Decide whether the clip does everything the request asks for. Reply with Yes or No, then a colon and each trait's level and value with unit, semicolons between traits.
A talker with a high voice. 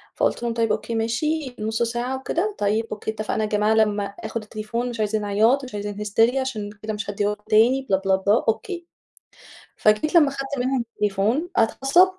Yes: high, 225 Hz